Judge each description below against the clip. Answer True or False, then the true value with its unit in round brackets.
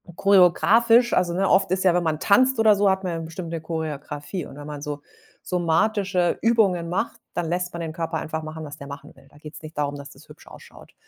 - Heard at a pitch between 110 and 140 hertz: False (170 Hz)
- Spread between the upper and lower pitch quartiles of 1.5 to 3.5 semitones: False (3.9 semitones)